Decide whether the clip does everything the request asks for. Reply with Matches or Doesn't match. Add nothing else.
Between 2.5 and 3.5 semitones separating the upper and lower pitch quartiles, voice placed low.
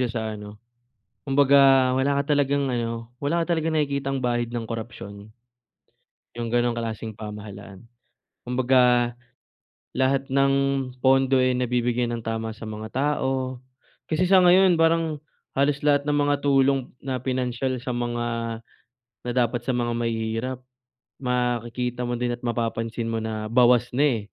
Matches